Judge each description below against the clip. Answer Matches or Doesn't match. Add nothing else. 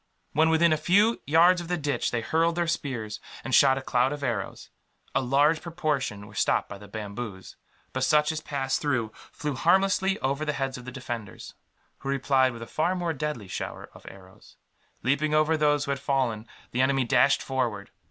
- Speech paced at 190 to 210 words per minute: Matches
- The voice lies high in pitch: Doesn't match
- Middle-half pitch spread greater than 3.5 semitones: Matches